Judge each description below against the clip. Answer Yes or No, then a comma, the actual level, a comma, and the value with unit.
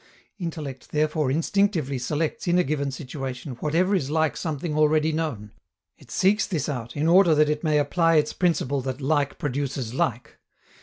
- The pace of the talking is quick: No, average, 165 wpm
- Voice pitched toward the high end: No, medium, 150 Hz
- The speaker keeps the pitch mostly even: No, average, 3.1 semitones